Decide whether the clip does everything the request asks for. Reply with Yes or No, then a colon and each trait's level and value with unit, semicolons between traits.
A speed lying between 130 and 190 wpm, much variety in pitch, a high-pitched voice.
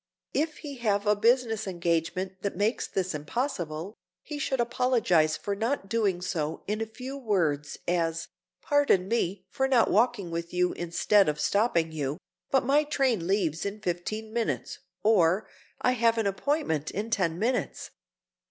Yes: average, 150 wpm; wide, 5.7 semitones; high, 200 Hz